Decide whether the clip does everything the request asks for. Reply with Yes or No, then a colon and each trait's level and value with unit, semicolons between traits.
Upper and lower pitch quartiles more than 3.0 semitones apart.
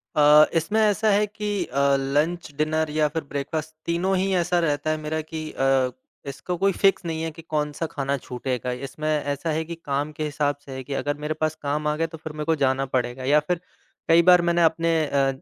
No: average, 2.7 semitones